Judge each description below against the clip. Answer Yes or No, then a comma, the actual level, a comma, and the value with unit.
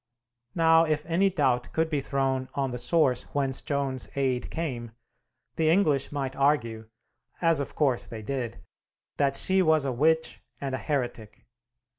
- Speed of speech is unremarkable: Yes, average, 155 wpm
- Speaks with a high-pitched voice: No, medium, 140 Hz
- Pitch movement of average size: Yes, average, 3.5 semitones